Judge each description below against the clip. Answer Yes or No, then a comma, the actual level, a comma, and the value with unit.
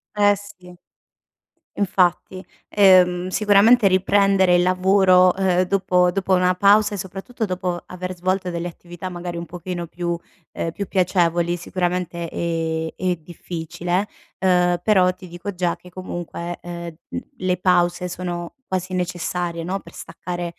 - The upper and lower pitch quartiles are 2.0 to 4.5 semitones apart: No, narrow, 1.4 semitones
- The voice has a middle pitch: Yes, medium, 180 Hz